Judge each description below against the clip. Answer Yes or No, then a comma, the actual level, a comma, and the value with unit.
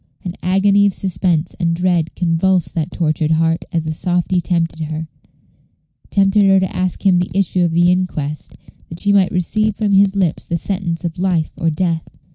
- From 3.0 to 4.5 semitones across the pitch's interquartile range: No, narrow, 2.5 semitones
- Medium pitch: Yes, medium, 175 Hz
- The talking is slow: No, average, 185 wpm